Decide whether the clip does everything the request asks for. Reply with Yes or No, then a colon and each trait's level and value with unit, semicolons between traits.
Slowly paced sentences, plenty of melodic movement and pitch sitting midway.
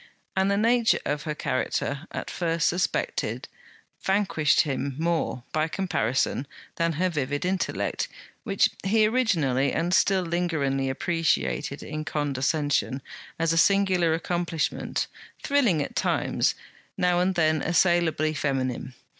No: slow, 120 wpm; average, 4.3 semitones; medium, 165 Hz